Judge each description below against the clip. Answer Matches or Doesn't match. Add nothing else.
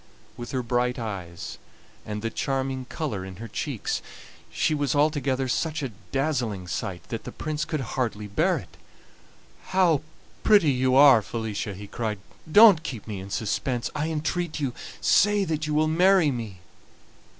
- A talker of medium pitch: Doesn't match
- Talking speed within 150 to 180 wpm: Matches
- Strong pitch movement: Matches